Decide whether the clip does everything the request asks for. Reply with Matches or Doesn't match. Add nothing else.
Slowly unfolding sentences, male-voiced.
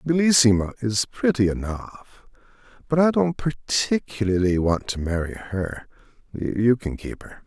Matches